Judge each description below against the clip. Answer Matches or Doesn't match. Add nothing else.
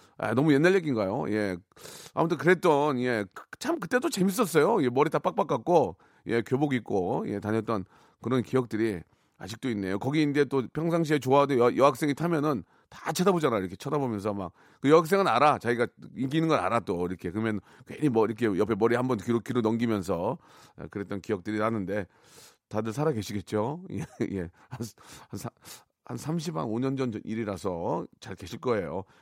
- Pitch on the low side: Matches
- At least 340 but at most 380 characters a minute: Matches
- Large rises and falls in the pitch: Matches